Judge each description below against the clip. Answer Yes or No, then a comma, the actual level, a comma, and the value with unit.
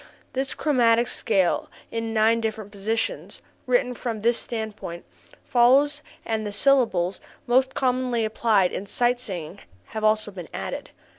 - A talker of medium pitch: No, high, 225 Hz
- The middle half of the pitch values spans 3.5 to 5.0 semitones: No, average, 3.1 semitones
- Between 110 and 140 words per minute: Yes, slow, 135 wpm